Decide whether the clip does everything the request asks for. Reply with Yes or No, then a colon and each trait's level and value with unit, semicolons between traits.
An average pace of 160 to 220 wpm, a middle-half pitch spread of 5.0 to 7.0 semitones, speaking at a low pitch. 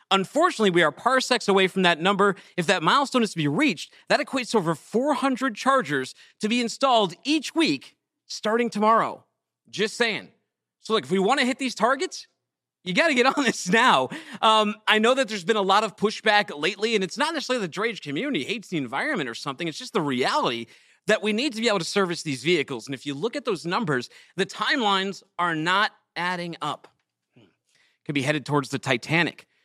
No: fast, 205 wpm; wide, 5.6 semitones; high, 210 Hz